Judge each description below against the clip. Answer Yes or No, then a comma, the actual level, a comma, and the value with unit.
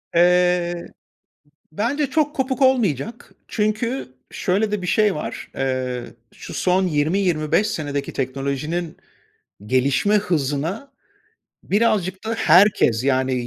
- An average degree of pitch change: No, wide, 7.3 semitones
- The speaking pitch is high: No, medium, 180 Hz